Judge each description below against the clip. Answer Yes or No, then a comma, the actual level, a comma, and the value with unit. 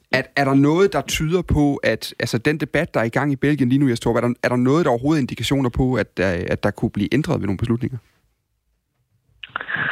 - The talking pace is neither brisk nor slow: No, fast, 240 wpm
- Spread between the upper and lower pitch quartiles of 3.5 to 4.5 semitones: Yes, average, 4.0 semitones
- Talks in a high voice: No, low, 125 Hz